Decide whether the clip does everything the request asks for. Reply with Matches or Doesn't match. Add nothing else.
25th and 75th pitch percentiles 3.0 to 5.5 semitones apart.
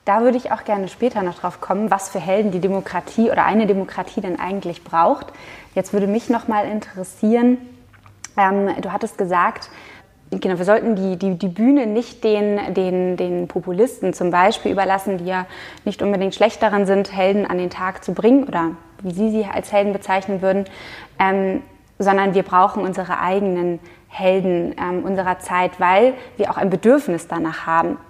Doesn't match